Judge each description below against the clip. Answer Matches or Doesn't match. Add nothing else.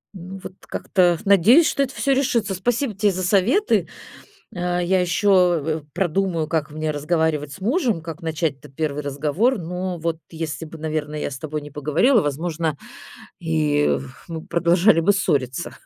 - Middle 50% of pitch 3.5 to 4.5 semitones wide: Matches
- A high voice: Doesn't match